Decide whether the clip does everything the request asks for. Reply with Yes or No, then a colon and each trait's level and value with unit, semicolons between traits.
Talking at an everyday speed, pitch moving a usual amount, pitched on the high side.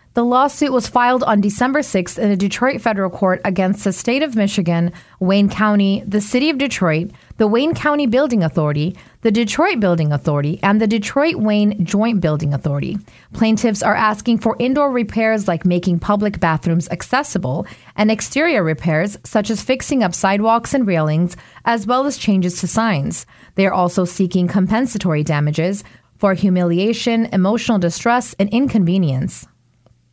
Yes: average, 155 wpm; average, 4.7 semitones; high, 205 Hz